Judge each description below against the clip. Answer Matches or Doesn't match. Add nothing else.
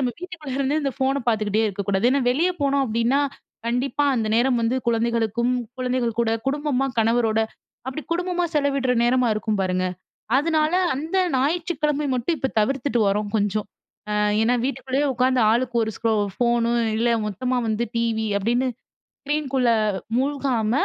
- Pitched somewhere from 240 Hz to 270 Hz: Matches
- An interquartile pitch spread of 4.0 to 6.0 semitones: Doesn't match